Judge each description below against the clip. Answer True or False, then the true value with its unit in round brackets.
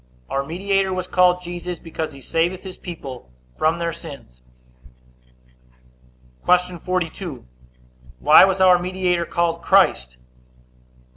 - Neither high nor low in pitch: True (175 Hz)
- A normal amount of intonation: False (2.1 semitones)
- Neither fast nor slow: False (120 wpm)